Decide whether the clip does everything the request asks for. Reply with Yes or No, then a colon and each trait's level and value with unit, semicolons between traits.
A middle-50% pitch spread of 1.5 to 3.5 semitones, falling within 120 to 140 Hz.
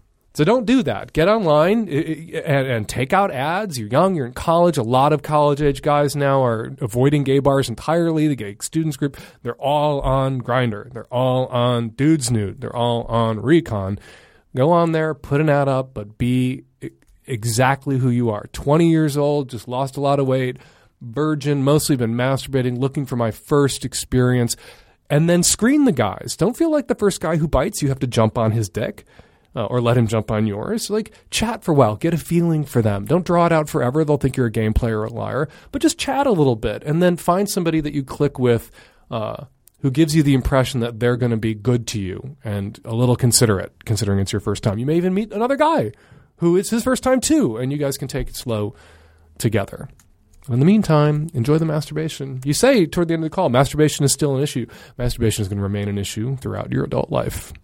No: average, 5.1 semitones; low, 135 Hz